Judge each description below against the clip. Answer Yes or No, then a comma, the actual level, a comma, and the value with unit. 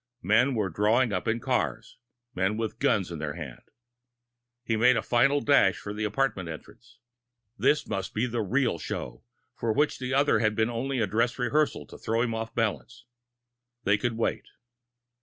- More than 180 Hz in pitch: No, low, 115 Hz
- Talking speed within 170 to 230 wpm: Yes, average, 175 wpm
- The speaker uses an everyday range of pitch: Yes, average, 3.3 semitones